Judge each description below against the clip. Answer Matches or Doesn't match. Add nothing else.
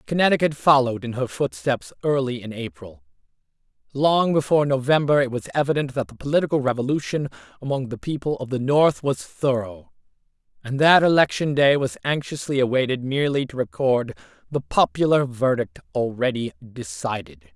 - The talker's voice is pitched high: Doesn't match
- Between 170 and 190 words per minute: Doesn't match